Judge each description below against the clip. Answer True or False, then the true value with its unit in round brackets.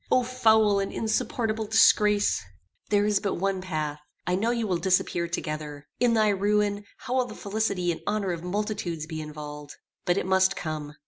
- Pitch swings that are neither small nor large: True (4.2 semitones)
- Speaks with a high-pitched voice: True (195 Hz)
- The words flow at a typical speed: True (180 wpm)